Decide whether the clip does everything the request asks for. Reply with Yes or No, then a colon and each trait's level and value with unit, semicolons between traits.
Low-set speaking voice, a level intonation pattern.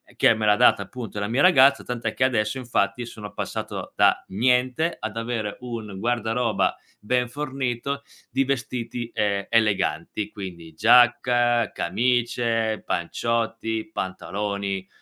No: low, 115 Hz; average, 3.0 semitones